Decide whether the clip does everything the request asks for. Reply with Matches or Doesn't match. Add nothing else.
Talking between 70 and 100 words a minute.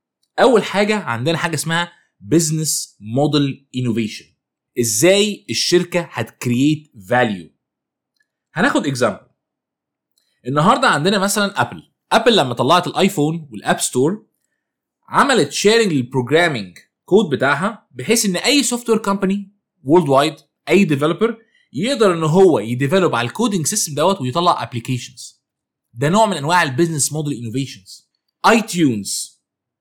Doesn't match